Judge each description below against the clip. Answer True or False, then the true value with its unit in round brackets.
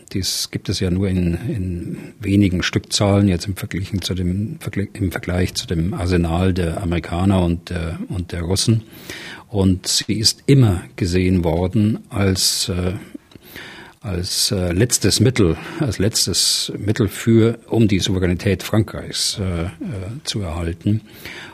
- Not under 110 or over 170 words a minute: True (130 wpm)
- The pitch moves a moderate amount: True (3.2 semitones)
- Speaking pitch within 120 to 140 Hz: False (95 Hz)